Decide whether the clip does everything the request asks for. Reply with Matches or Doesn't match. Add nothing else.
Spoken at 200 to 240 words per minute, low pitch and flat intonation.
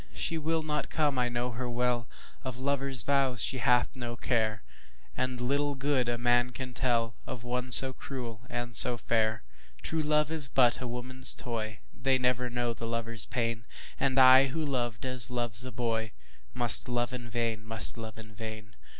Doesn't match